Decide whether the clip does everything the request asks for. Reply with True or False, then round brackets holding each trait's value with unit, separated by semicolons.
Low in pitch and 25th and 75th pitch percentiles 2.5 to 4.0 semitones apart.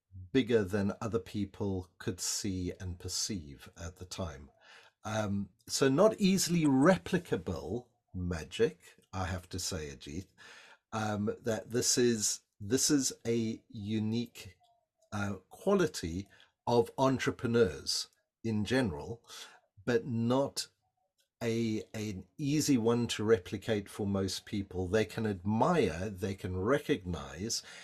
False (110 Hz; 4.4 semitones)